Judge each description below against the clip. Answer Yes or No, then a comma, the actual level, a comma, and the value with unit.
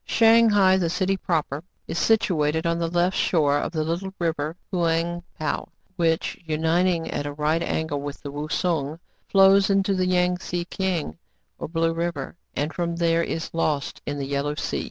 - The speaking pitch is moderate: Yes, medium, 165 Hz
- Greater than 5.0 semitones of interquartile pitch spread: No, average, 2.9 semitones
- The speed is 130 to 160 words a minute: No, average, 180 wpm